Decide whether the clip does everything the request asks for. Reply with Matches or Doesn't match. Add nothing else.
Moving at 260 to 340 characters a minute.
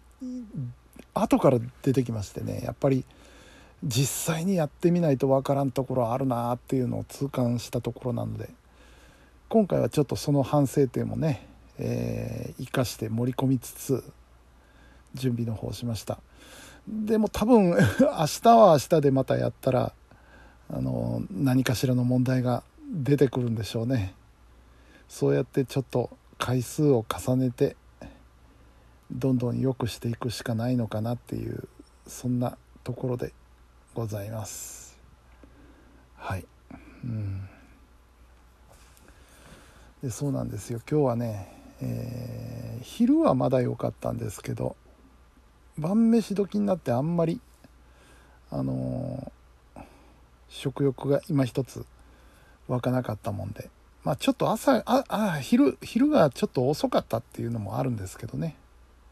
Matches